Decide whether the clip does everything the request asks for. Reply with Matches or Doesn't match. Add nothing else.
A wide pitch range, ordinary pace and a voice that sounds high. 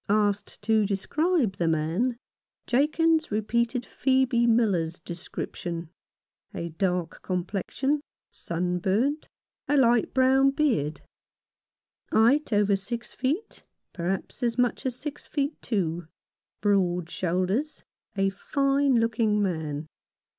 Doesn't match